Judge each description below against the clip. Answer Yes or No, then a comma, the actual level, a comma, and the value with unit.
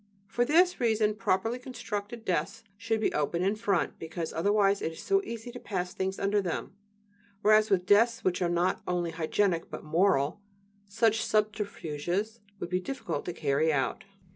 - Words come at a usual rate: Yes, average, 165 wpm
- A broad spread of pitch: No, average, 4.2 semitones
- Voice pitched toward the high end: Yes, high, 200 Hz